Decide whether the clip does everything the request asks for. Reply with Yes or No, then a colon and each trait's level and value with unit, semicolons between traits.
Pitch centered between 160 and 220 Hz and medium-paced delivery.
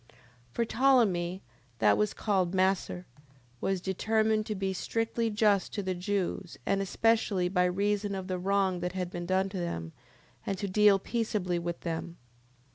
Yes: high, 190 Hz; average, 160 wpm